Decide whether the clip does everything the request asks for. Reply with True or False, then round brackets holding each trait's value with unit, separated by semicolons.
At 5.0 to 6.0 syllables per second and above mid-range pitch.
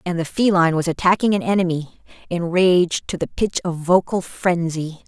False (5.5 syllables/s; 175 Hz)